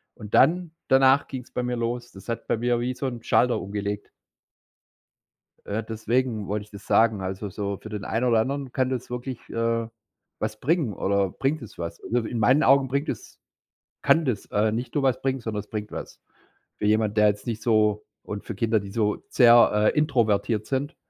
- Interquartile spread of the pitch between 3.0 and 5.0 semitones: Yes, average, 3.4 semitones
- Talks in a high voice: No, low, 115 Hz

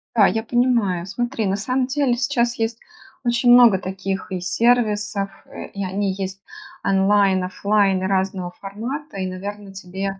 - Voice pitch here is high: Yes, high, 200 Hz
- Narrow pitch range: No, average, 3.7 semitones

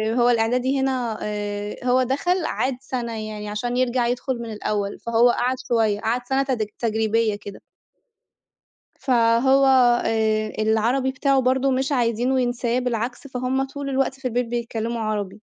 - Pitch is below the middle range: No, high, 240 Hz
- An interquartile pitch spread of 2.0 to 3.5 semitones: Yes, average, 2.8 semitones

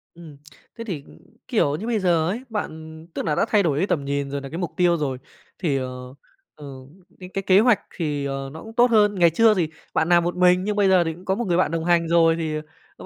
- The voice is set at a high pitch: No, medium, 170 Hz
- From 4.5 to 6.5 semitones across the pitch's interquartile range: No, average, 4.0 semitones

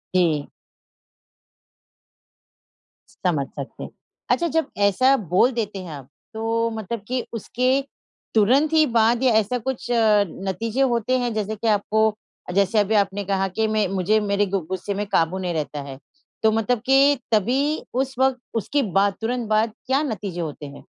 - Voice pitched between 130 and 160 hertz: No, high, 215 Hz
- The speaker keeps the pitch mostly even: No, average, 3.8 semitones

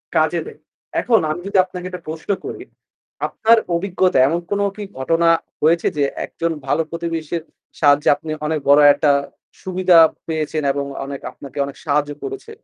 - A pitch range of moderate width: Yes, average, 3.6 semitones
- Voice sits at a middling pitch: Yes, medium, 165 Hz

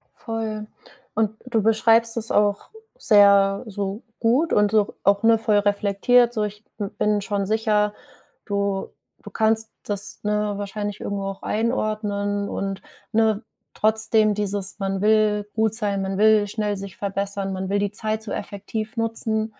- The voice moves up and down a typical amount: No, narrow, 1.5 semitones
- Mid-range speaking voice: No, high, 210 Hz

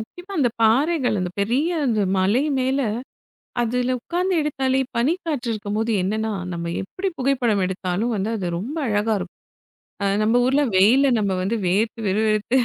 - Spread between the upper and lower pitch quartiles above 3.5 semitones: Yes, average, 4.5 semitones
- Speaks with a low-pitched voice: No, high, 230 Hz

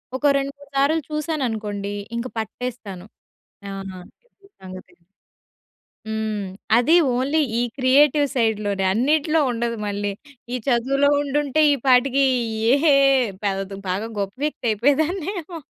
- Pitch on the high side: Yes, very high, 255 Hz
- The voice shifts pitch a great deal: Yes, wide, 5.8 semitones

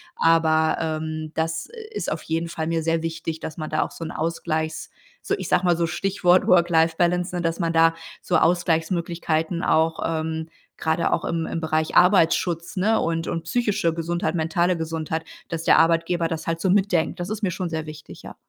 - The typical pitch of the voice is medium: Yes, medium, 165 Hz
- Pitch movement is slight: Yes, narrow, 1.4 semitones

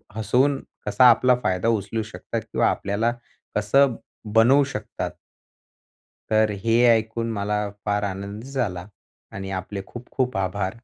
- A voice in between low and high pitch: No, low, 110 Hz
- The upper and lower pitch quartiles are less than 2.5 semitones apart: No, average, 2.8 semitones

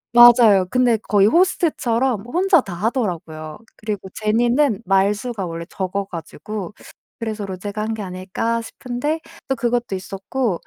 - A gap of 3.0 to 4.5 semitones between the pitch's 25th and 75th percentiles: Yes, average, 4.0 semitones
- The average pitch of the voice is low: No, high, 215 Hz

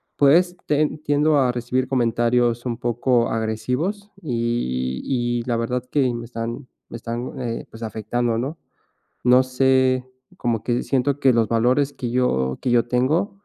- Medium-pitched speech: No, low, 125 Hz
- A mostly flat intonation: Yes, narrow, 2.2 semitones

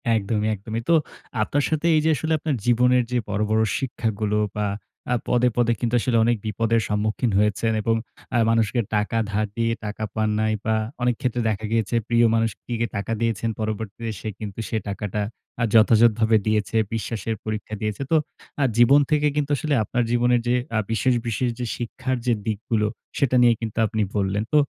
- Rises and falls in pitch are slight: Yes, narrow, 2.2 semitones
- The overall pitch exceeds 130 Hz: No, low, 115 Hz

